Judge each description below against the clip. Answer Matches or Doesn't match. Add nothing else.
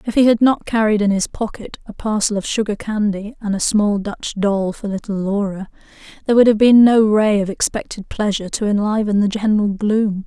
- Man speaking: Doesn't match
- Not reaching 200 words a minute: Doesn't match